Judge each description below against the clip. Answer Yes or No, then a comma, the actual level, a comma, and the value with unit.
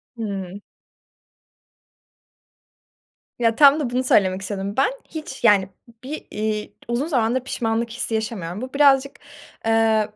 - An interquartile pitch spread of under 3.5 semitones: No, average, 3.9 semitones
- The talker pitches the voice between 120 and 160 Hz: No, high, 225 Hz